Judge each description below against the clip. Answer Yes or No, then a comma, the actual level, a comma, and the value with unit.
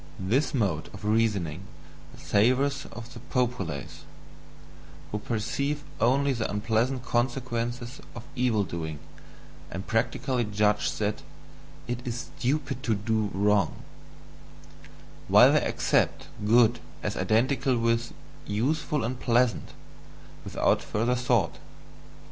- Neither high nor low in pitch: No, low, 115 Hz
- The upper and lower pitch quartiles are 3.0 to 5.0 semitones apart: Yes, average, 3.3 semitones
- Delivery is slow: Yes, slow, 110 wpm